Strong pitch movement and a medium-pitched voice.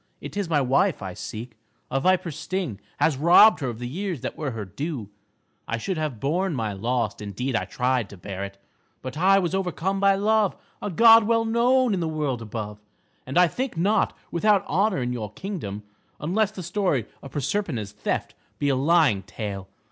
Yes: wide, 8.8 semitones; medium, 150 Hz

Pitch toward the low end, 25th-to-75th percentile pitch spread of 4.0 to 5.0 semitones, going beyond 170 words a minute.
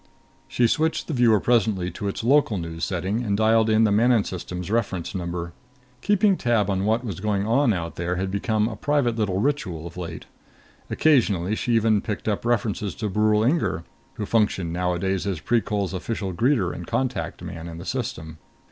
Yes: low, 105 Hz; average, 4.3 semitones; average, 185 wpm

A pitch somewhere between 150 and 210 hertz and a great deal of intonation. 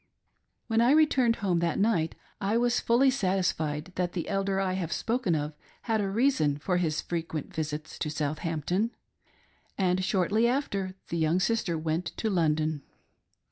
Yes: medium, 185 Hz; wide, 5.8 semitones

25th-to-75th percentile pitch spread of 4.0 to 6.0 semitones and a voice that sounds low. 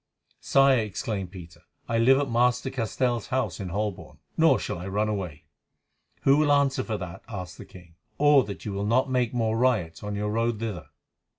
Yes: average, 4.7 semitones; low, 110 Hz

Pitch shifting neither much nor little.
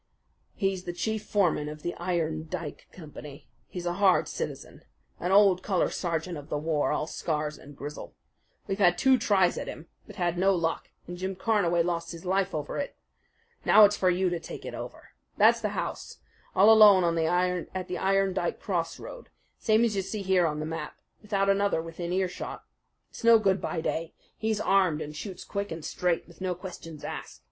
Yes: average, 3.0 semitones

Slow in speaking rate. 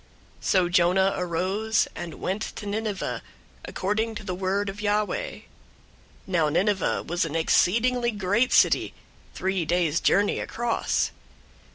Yes: slow, 130 wpm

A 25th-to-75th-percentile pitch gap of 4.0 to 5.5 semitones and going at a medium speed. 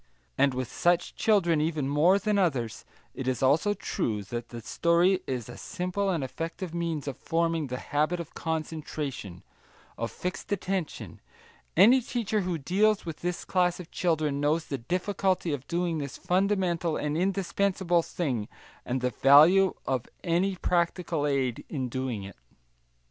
Yes: average, 4.9 semitones; average, 155 wpm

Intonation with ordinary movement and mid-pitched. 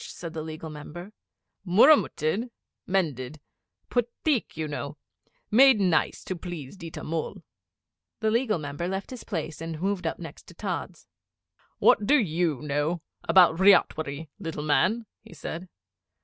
Yes: average, 4.4 semitones; medium, 170 Hz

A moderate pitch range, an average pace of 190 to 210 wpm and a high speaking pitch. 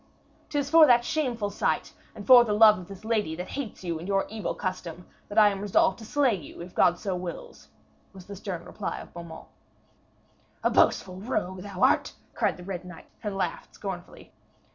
Yes: average, 3.9 semitones; average, 195 wpm; high, 200 Hz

